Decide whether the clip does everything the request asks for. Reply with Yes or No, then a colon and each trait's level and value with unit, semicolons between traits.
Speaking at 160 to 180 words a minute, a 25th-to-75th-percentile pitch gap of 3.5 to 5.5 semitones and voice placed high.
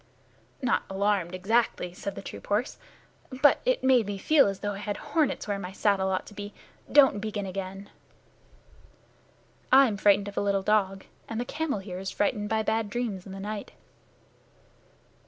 No: average, 175 wpm; narrow, 2.5 semitones; high, 205 Hz